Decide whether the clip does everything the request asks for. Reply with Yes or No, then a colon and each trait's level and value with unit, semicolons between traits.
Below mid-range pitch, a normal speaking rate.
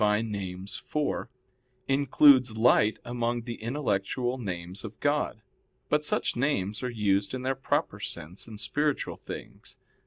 No: low, 115 Hz; slow, 130 wpm